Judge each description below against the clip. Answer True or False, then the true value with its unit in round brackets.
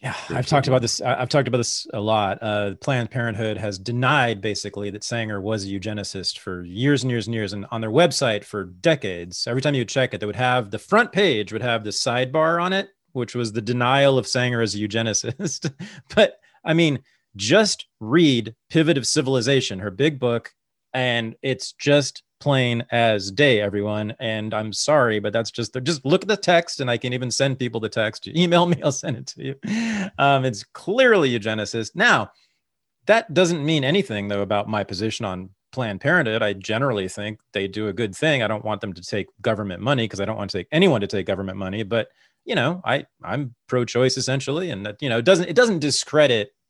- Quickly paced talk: True (210 wpm)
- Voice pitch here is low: True (120 Hz)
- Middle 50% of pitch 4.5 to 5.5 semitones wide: True (5.2 semitones)